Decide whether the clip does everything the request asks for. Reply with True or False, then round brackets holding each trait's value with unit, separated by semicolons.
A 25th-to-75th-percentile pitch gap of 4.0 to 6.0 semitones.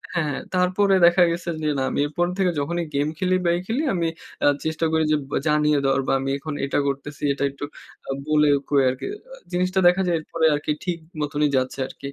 False (3.5 semitones)